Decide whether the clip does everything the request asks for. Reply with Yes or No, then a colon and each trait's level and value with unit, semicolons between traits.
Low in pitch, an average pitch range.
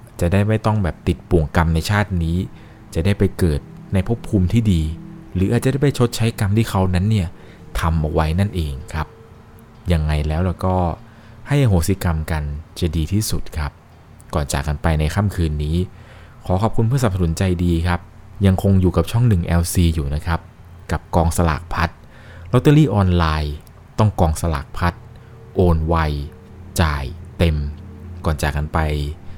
Yes: very low, 90 Hz; average, 4.2 semitones